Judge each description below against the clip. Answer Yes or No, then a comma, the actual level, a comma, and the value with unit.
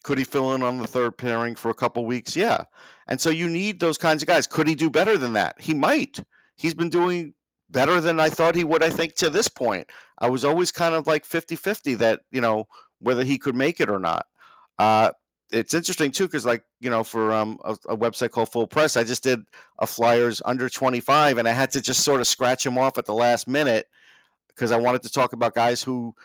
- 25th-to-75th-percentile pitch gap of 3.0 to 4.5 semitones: No, average, 5.1 semitones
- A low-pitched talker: Yes, low, 125 Hz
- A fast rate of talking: Yes, fast, 240 wpm